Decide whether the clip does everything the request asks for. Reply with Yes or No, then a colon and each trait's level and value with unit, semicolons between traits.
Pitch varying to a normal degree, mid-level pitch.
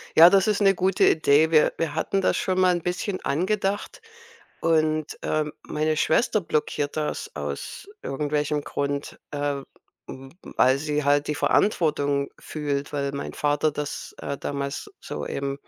Yes: average, 3.5 semitones; medium, 150 Hz